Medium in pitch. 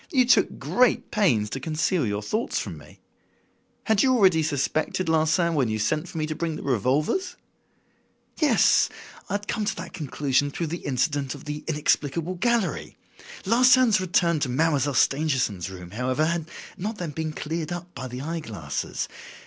Yes: medium, 155 Hz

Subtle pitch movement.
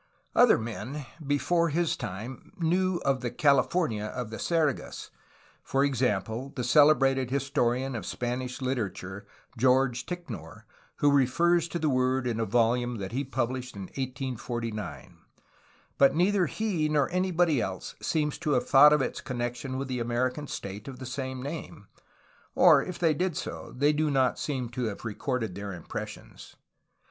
No: average, 3.8 semitones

